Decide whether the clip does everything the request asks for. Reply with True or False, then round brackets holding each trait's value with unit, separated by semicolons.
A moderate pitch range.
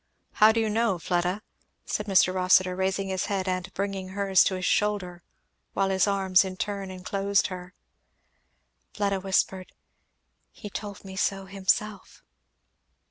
False (1.4 semitones)